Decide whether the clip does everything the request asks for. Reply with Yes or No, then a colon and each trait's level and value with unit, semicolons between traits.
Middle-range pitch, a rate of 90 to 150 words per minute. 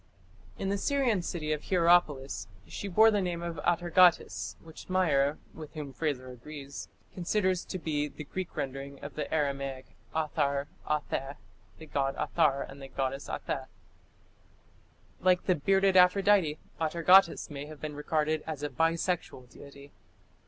Yes: medium, 155 Hz; average, 145 wpm